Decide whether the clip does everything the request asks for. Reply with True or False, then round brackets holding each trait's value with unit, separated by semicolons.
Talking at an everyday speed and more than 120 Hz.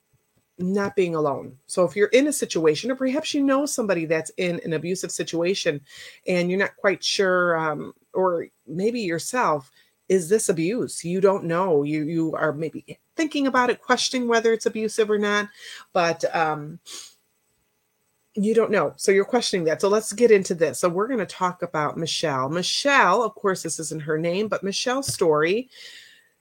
True (175 wpm; 190 Hz)